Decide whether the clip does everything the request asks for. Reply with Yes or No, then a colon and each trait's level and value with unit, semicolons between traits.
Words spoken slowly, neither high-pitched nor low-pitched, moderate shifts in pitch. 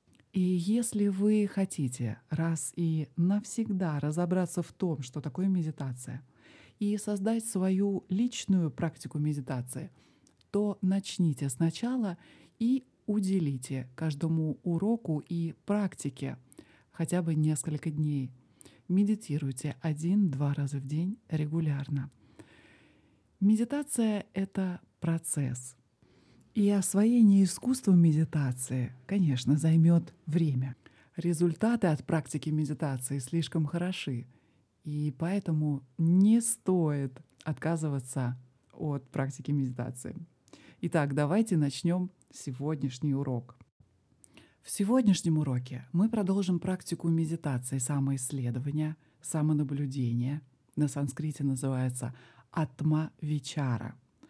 Yes: slow, 90 wpm; medium, 155 Hz; average, 5.0 semitones